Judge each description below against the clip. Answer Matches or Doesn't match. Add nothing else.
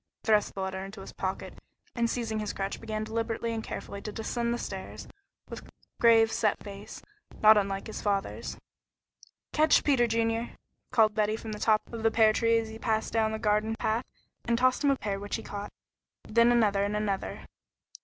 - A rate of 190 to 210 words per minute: Matches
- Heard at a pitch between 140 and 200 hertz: Doesn't match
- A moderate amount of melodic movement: Doesn't match